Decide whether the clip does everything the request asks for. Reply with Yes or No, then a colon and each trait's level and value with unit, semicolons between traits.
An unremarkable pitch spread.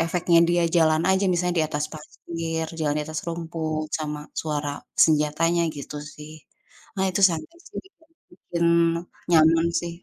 No: narrow, 1.8 semitones